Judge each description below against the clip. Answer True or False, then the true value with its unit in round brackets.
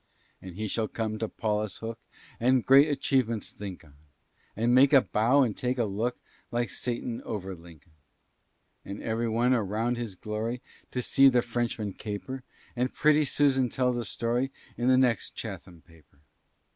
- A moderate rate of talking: True (165 wpm)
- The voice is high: False (115 Hz)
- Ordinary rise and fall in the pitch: True (3.1 semitones)